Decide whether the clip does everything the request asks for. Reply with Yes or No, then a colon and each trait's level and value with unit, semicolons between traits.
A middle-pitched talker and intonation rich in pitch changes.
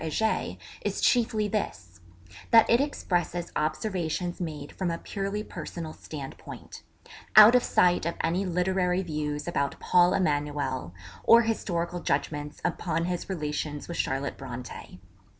No: medium, 170 Hz; average, 4.4 semitones